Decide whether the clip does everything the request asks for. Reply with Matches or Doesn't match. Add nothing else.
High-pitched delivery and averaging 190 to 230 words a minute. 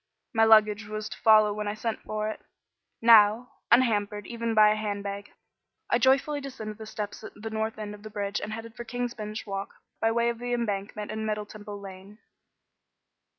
Matches